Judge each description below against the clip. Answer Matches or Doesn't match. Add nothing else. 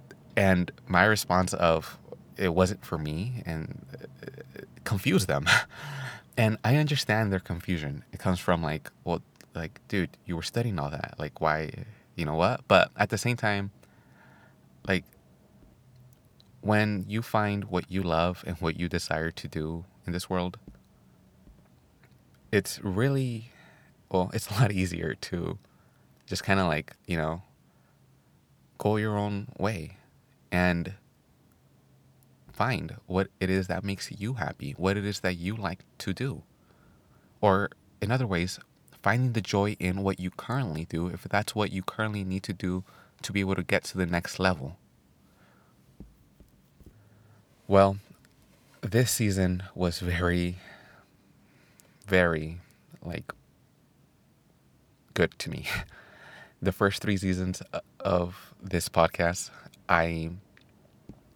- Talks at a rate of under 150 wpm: Matches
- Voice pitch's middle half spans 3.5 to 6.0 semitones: Doesn't match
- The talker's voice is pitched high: Doesn't match